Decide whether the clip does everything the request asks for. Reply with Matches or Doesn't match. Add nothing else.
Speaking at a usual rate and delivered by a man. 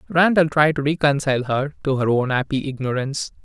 Matches